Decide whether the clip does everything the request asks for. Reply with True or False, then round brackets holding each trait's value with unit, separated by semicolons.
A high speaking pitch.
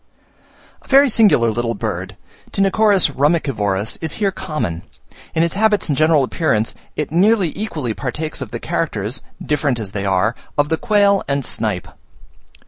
False (150 Hz)